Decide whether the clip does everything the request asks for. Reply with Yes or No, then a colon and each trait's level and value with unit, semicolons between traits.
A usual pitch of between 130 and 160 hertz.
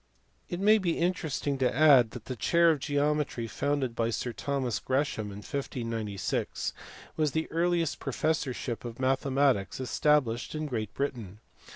Yes: low, 135 Hz